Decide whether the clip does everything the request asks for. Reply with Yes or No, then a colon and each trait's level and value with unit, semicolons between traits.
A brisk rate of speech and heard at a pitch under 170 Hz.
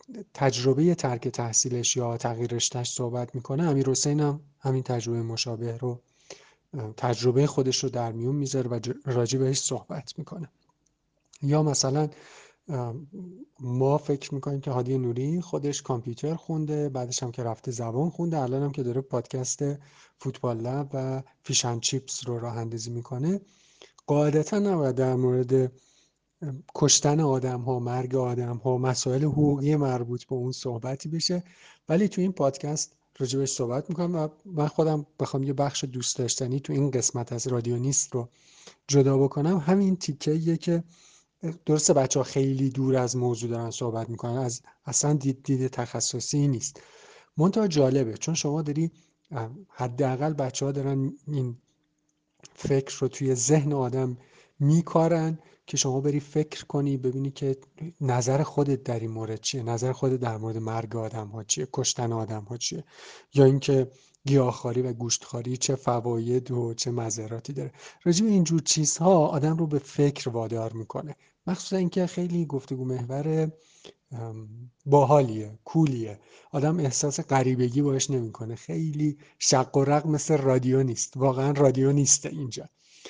Yes: fast, 145 wpm; low, 135 Hz